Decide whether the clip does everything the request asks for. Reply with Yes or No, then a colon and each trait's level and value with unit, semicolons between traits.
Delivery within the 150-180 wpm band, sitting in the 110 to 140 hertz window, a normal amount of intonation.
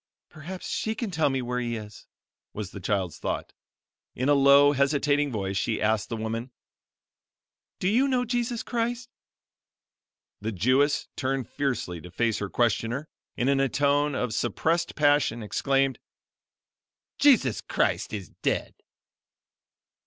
No: average, 140 wpm; low, 135 Hz; average, 5.0 semitones